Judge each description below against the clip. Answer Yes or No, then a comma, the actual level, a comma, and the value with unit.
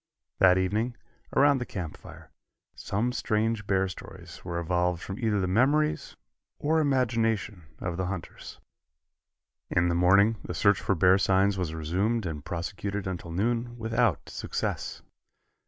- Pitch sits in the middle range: No, low, 100 Hz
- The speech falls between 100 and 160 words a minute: Yes, average, 140 wpm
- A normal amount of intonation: Yes, average, 4.3 semitones